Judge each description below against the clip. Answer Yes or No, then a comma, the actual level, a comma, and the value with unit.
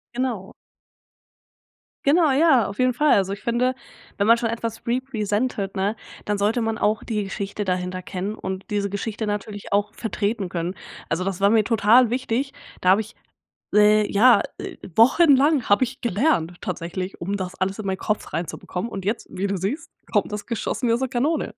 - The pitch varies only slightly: No, average, 3.5 semitones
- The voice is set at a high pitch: Yes, high, 210 Hz